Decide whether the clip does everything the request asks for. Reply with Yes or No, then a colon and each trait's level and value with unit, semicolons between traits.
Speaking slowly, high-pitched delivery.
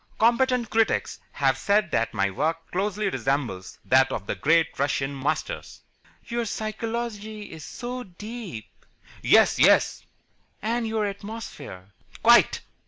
Yes: slow, 120 wpm; high, 200 Hz